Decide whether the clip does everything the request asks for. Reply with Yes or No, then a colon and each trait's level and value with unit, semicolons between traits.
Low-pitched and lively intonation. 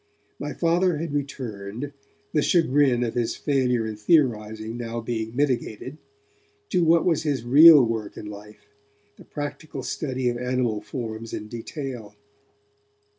No: low, 125 Hz; average, 4.6 semitones